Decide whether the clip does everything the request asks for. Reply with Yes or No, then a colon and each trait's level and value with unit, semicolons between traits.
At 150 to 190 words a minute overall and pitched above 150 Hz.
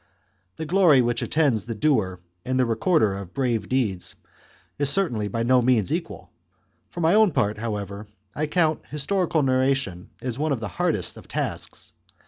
No: average, 165 wpm; low, 130 Hz